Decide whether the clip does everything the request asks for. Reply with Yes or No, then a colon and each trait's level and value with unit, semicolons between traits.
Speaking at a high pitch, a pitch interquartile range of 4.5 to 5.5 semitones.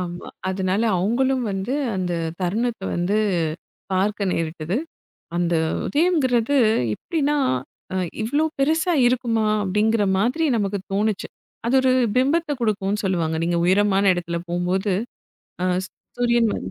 Yes: high, 205 Hz; average, 5.2 semitones